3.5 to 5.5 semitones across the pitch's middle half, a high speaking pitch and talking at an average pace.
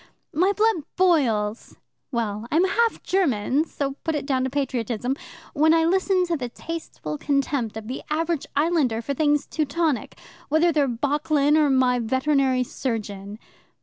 Yes: average, 4.7 semitones; very high, 280 Hz; average, 150 wpm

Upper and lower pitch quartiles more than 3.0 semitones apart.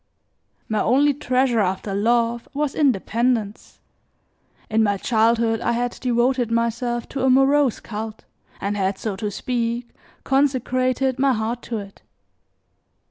No: average, 2.7 semitones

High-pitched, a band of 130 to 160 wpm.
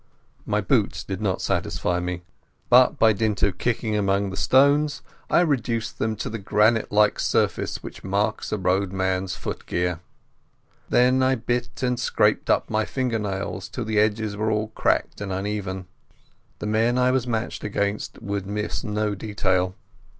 No: low, 105 Hz; average, 155 wpm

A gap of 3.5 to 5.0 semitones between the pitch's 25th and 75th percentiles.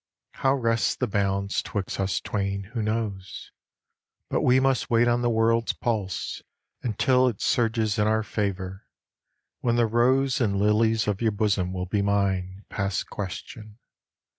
No: average, 3.0 semitones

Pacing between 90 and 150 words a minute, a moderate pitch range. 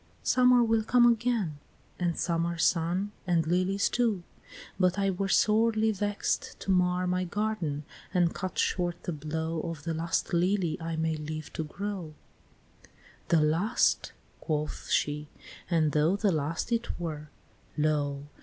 Yes: average, 145 wpm; average, 4.2 semitones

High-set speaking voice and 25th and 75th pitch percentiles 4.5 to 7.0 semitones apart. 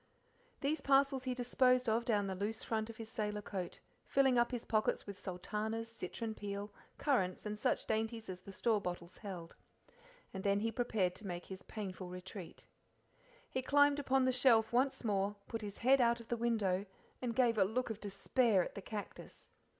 No: high, 220 Hz; average, 3.6 semitones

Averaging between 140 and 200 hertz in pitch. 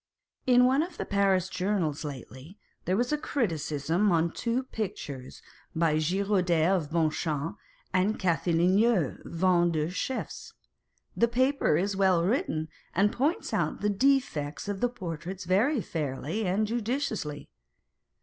Yes: medium, 185 Hz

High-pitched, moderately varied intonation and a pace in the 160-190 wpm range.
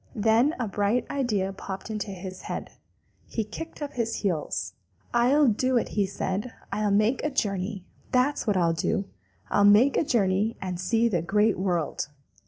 Yes: high, 210 Hz; average, 3.9 semitones; average, 170 wpm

